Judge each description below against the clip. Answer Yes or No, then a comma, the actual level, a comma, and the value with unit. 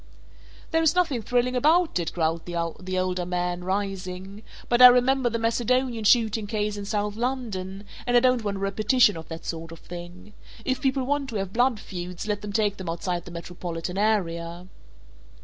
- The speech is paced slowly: No, average, 185 wpm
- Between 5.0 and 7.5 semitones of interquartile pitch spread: Yes, average, 5.3 semitones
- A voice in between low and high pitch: No, high, 205 Hz